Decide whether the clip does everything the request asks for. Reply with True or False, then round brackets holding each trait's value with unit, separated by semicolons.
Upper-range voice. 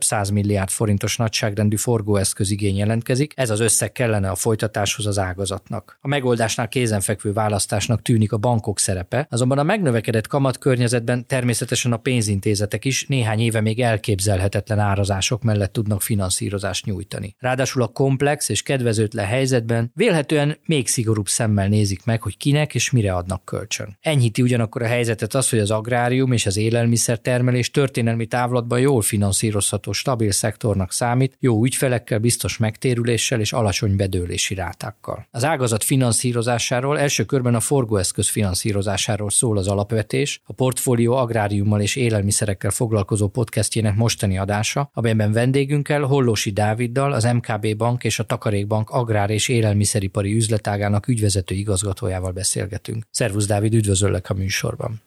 False (115 Hz)